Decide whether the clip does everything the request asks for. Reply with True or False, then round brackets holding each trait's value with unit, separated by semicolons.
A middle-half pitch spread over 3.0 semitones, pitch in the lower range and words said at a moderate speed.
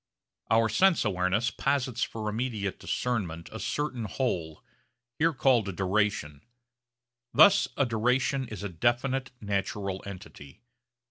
False (4.6 semitones; 110 Hz; 120 wpm)